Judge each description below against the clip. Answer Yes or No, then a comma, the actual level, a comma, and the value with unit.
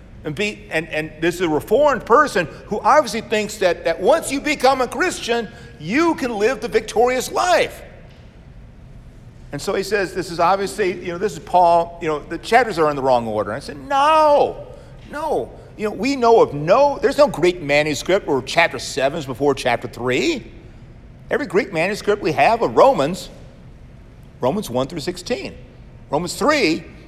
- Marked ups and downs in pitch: Yes, wide, 7.8 semitones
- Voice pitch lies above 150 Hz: Yes, medium, 185 Hz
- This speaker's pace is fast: No, average, 180 wpm